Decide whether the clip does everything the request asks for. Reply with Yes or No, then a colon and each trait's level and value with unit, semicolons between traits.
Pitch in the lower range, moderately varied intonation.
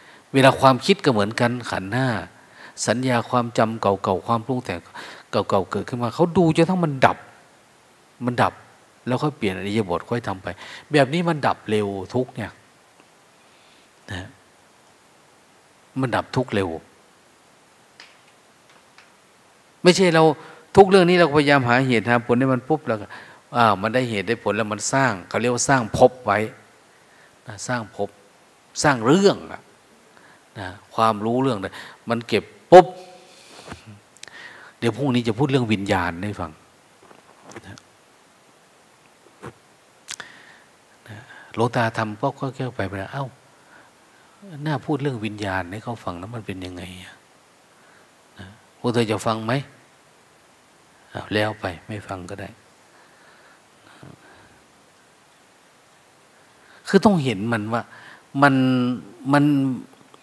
Yes: low, 120 Hz; average, 4.7 semitones